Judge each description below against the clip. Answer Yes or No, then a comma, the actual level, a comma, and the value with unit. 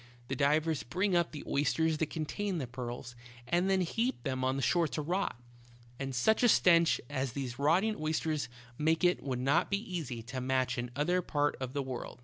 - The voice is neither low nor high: Yes, medium, 150 Hz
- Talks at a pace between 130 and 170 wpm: No, fast, 205 wpm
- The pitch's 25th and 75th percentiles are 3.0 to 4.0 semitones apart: No, average, 4.9 semitones